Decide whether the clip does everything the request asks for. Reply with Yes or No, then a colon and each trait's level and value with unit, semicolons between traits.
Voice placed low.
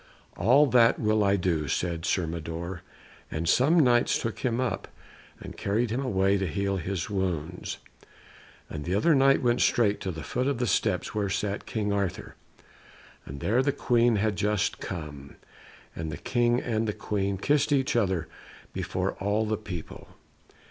Yes: low, 100 Hz